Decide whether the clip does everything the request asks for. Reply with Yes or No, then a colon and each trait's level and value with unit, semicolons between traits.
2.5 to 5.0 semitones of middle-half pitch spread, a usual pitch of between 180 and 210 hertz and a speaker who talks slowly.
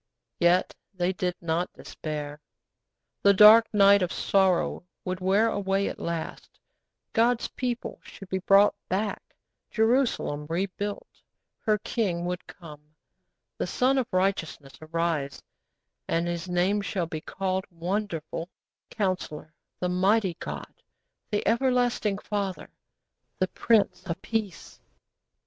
Yes: average, 3.3 semitones; high, 190 Hz; slow, 120 wpm